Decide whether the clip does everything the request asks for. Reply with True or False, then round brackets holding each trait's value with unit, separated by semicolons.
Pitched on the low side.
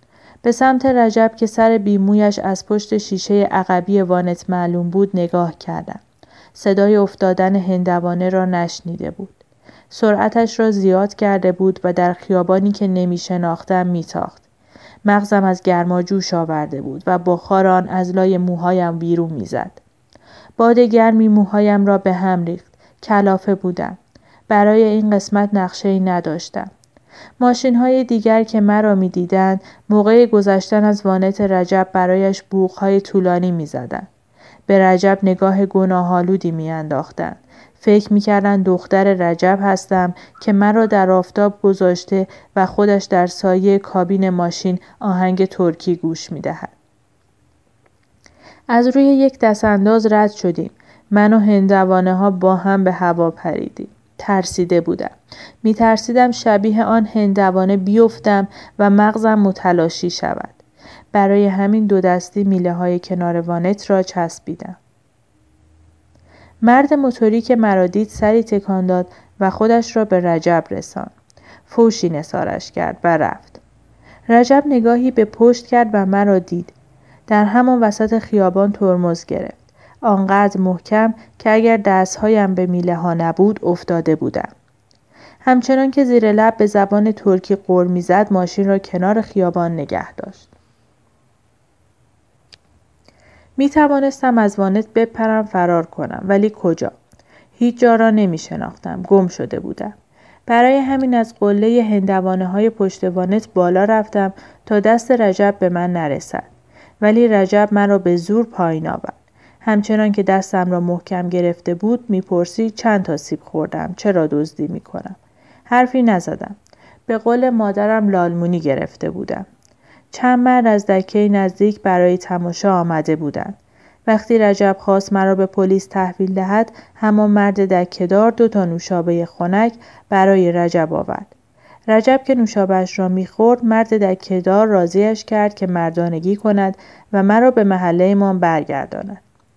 False (195 Hz)